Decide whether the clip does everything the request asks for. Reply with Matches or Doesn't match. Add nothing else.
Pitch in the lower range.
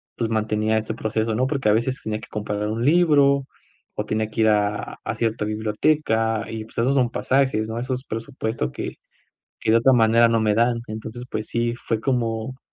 Matches